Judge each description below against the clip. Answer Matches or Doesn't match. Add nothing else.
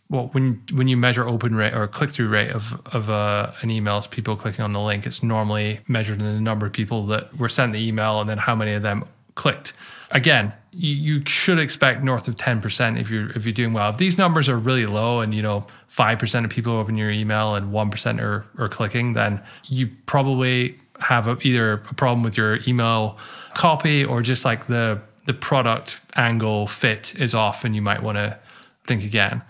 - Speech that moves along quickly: Matches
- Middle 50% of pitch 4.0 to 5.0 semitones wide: Doesn't match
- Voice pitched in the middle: Doesn't match